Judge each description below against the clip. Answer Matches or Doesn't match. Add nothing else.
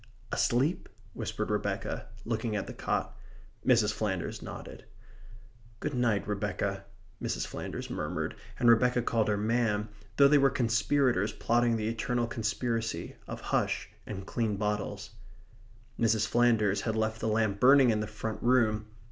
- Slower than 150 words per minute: Matches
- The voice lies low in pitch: Matches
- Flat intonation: Matches